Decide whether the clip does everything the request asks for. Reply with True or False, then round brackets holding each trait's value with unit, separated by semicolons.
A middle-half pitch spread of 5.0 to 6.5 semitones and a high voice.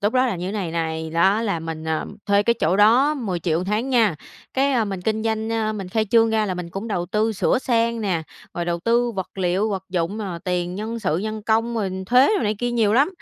False (4.1 semitones; 210 Hz)